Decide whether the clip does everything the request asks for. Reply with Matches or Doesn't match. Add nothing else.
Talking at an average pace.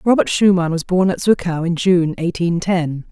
Matches